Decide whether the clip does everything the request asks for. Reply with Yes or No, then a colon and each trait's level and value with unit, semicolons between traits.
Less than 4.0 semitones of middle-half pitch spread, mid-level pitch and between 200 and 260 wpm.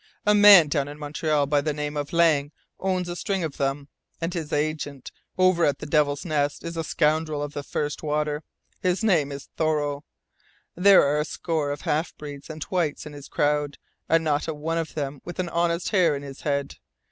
Yes: narrow, 2.5 semitones; medium, 150 Hz; fast, 205 wpm